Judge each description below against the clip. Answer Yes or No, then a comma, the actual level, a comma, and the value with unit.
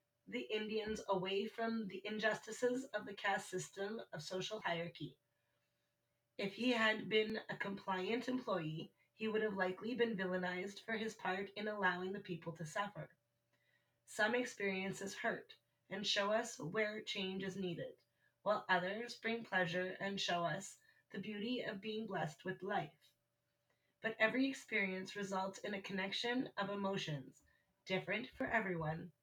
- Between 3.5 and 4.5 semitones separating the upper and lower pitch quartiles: No, average, 2.8 semitones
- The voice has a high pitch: Yes, high, 200 Hz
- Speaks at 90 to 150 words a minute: Yes, average, 145 wpm